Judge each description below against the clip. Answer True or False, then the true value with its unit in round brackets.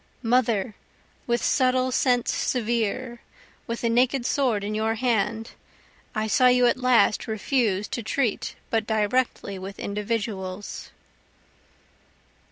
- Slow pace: True (115 wpm)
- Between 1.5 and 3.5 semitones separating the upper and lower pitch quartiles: True (2.9 semitones)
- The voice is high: True (230 Hz)